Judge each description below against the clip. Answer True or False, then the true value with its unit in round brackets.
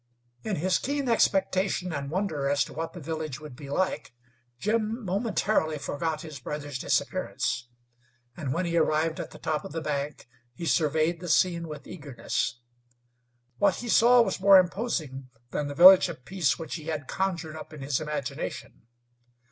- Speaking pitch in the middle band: True (160 Hz)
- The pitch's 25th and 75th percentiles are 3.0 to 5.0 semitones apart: True (4.3 semitones)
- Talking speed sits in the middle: True (170 wpm)